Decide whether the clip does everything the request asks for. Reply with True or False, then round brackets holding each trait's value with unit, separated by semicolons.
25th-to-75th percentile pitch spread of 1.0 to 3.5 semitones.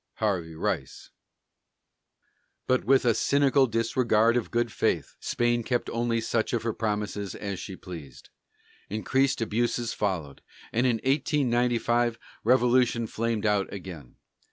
True (2.8 semitones)